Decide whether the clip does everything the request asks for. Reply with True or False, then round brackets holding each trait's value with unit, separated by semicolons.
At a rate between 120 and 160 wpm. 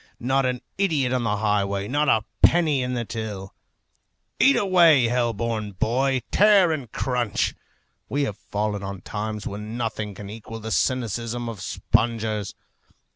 True (150 wpm)